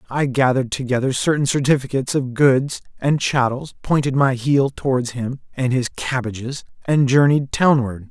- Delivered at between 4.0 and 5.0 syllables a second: Yes, 4.9 syllables/s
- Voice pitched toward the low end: Yes, low, 130 Hz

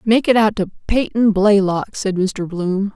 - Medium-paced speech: Yes, average, 185 wpm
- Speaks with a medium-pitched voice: No, high, 205 Hz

